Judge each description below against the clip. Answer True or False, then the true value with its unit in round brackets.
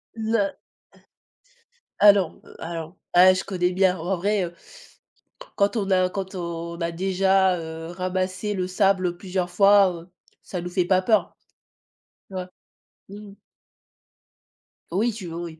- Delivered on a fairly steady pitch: True (1.9 semitones)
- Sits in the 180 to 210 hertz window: True (185 Hz)